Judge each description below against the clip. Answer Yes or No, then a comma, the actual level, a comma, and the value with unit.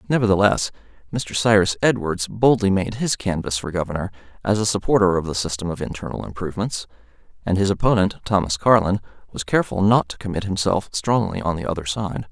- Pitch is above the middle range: No, very low, 95 Hz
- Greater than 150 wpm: Yes, average, 170 wpm